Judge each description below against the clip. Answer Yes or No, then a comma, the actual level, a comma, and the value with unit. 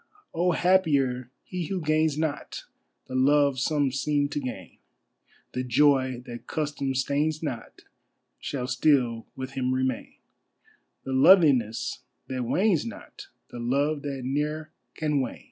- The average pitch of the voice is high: No, medium, 140 Hz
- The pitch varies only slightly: No, average, 3.1 semitones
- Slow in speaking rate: Yes, slow, 130 wpm